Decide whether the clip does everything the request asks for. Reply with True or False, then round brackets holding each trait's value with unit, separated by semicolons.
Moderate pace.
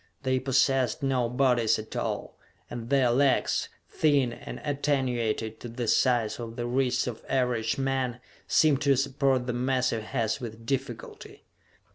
True (145 wpm)